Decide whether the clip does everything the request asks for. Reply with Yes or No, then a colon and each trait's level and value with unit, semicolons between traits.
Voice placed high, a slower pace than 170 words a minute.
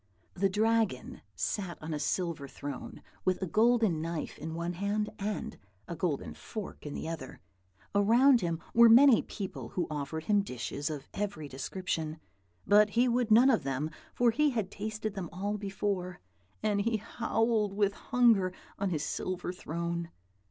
Yes: high, 195 Hz; average, 160 wpm